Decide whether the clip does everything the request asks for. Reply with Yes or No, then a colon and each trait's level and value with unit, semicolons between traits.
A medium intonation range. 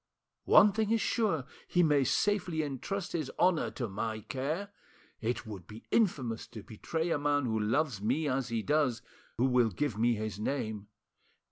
No: wide, 6.2 semitones